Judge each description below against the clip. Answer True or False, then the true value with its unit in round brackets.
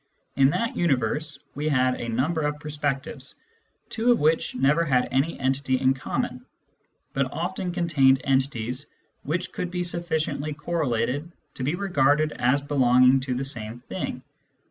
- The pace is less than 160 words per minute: True (145 wpm)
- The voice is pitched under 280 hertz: True (140 Hz)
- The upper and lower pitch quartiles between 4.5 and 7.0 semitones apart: False (3.4 semitones)